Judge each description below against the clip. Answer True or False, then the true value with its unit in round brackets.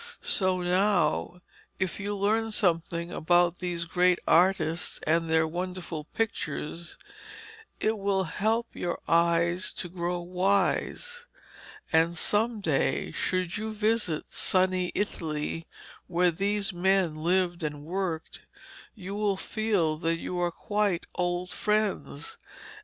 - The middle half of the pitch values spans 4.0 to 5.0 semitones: False (3.0 semitones)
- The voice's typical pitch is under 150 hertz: False (180 Hz)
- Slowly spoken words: True (120 wpm)